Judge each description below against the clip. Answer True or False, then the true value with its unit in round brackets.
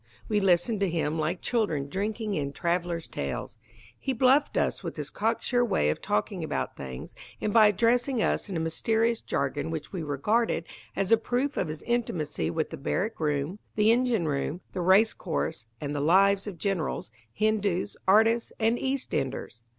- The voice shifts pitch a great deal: True (6.3 semitones)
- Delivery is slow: False (175 wpm)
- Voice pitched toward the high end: True (195 Hz)